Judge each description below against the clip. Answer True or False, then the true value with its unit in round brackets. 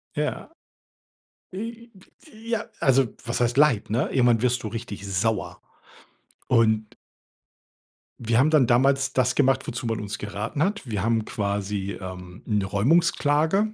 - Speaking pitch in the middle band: False (120 Hz)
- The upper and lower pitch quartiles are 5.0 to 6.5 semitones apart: True (5.6 semitones)